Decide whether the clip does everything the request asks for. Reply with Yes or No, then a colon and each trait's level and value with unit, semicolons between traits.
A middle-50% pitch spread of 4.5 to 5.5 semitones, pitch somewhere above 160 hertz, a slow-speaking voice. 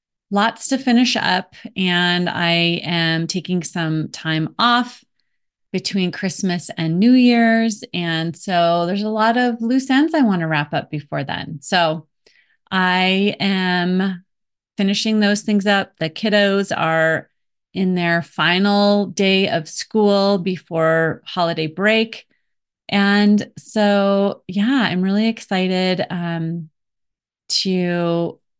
No: average, 3.5 semitones; medium, 185 Hz; slow, 120 wpm